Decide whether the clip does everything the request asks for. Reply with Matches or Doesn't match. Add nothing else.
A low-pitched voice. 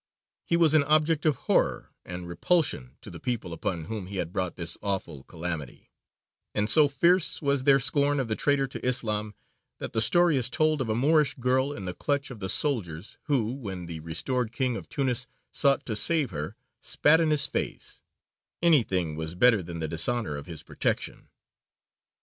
Matches